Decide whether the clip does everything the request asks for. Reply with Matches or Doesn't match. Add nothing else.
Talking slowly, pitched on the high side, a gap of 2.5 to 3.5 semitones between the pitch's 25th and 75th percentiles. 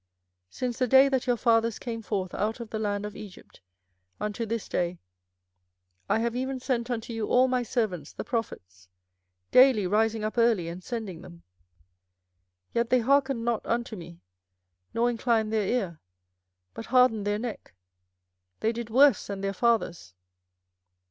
Doesn't match